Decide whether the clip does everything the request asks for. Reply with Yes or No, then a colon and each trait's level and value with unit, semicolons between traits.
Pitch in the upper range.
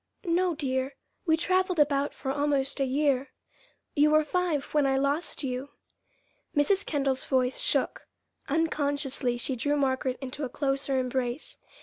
Yes: very high, 280 Hz